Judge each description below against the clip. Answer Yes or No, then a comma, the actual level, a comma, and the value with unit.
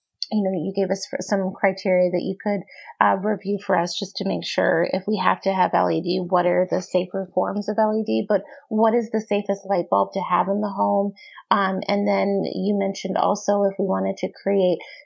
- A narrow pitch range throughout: Yes, narrow, 1.9 semitones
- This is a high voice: Yes, high, 195 Hz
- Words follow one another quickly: Yes, fast, 215 wpm